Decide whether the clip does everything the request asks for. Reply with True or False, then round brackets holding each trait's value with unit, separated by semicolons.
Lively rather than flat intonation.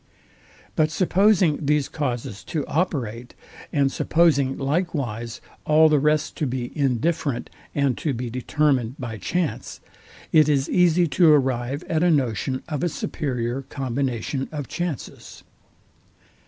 False (3.8 semitones)